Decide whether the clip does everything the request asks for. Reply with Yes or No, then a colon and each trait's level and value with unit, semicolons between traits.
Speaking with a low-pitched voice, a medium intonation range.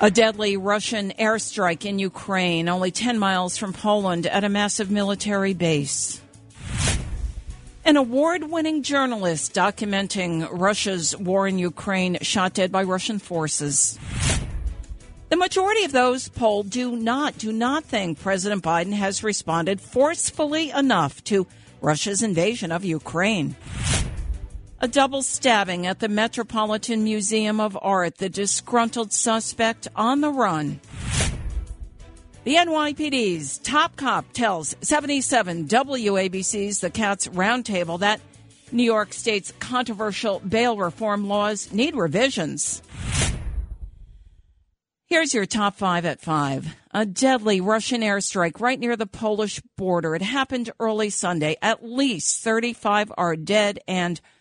No: high, 205 Hz; average, 4.7 semitones